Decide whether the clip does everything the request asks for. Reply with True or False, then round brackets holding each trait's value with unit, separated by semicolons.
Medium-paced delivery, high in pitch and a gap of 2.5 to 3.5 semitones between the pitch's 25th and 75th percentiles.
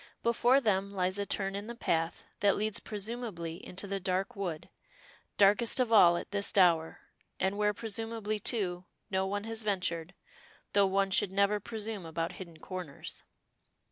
True (160 wpm; 200 Hz; 2.8 semitones)